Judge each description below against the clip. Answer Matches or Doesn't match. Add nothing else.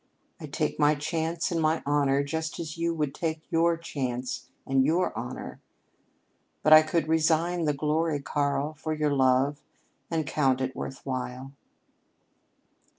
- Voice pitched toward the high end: Doesn't match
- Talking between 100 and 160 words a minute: Matches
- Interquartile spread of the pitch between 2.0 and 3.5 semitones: Matches